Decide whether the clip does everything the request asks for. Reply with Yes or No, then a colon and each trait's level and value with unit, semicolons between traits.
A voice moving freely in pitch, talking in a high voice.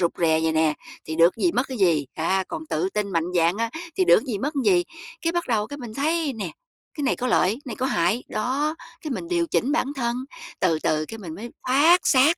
Yes: wide, 8.3 semitones; high, 225 Hz